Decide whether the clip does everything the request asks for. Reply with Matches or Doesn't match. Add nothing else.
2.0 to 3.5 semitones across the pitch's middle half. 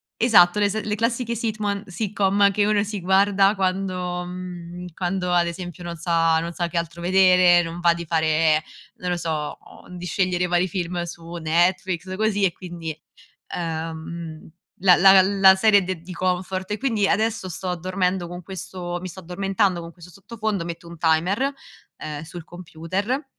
Matches